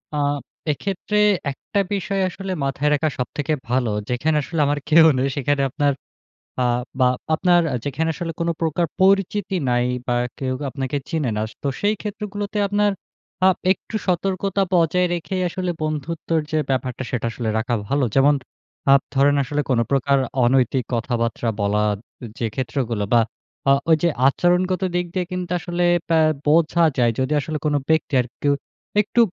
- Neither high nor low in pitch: Yes, medium, 150 Hz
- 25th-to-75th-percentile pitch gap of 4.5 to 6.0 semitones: Yes, average, 5.3 semitones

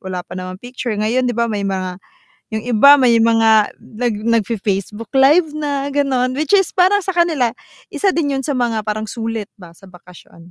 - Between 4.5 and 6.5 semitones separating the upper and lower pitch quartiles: Yes, average, 5.0 semitones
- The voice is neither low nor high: No, high, 235 Hz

